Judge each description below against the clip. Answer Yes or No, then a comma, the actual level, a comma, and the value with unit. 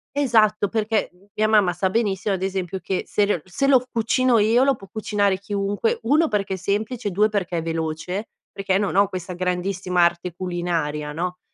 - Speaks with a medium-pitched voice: No, high, 195 Hz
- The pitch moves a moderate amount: Yes, average, 3.1 semitones